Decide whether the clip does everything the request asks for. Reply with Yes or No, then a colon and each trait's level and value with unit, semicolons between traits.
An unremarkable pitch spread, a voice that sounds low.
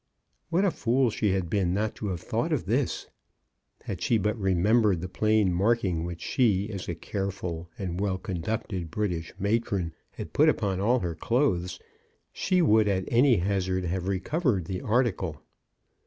Yes: average, 3.6 semitones; low, 100 Hz